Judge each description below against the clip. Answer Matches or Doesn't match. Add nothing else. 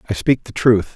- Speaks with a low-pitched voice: Matches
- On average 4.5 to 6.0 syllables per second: Matches